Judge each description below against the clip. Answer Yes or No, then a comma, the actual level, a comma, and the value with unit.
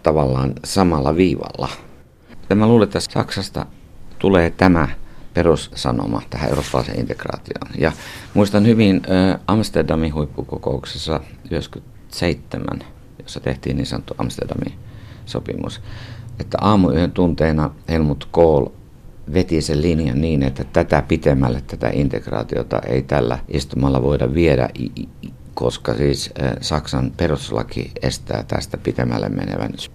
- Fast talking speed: No, average, 110 wpm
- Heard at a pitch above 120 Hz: No, very low, 80 Hz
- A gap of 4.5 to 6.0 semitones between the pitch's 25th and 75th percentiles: Yes, average, 5.3 semitones